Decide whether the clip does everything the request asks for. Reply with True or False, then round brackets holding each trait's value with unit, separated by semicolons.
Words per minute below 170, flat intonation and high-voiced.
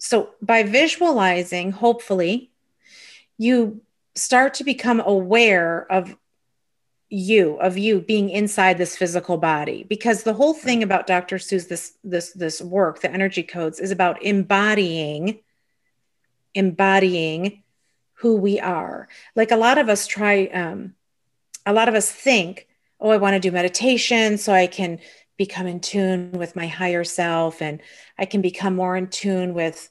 False (150 wpm; 3.4 semitones; 195 Hz)